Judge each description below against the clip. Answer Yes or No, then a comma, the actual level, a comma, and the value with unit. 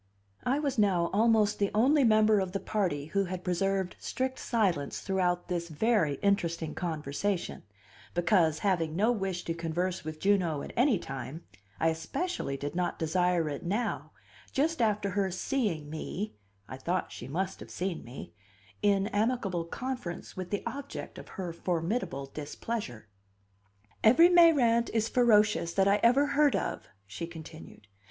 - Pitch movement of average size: Yes, average, 4.9 semitones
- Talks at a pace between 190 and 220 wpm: No, average, 150 wpm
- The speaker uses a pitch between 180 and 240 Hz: Yes, high, 190 Hz